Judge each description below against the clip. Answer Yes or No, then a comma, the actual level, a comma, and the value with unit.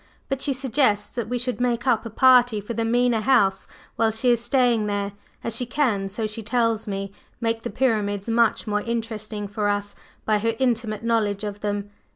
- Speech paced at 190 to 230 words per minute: Yes, average, 195 wpm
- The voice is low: No, high, 225 Hz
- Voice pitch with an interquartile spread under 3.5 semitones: Yes, average, 2.8 semitones